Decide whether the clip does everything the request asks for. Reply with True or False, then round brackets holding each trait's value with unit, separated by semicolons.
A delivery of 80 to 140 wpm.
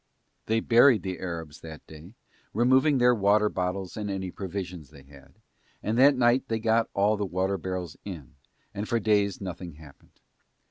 False (170 wpm)